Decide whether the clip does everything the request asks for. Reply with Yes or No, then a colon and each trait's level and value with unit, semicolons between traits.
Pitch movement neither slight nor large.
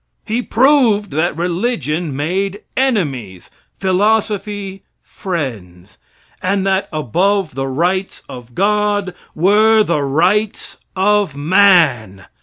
No: wide, 5.9 semitones